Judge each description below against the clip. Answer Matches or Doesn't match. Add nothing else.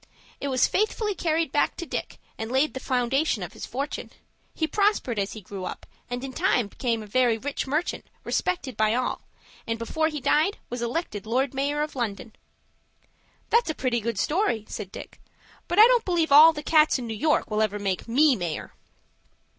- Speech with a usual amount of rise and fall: Doesn't match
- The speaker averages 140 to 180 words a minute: Doesn't match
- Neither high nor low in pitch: Doesn't match